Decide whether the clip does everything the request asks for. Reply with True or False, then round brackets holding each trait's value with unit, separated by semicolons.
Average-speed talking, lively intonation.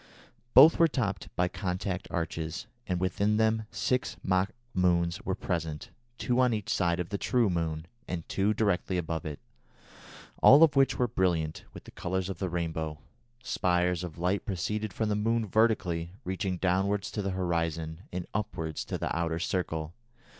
False (170 wpm; 3.6 semitones)